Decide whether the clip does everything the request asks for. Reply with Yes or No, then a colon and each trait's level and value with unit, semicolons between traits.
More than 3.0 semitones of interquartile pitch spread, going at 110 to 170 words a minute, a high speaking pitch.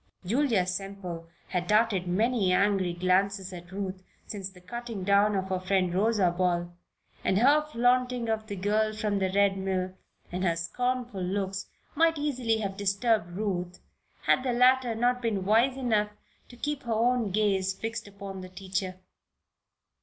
Yes: average, 3.8 semitones; average, 160 wpm; high, 200 Hz